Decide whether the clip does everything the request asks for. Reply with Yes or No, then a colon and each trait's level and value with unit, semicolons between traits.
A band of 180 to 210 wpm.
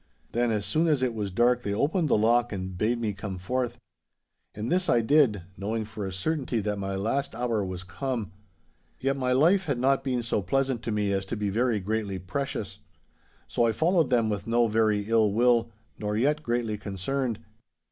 Yes: average, 200 wpm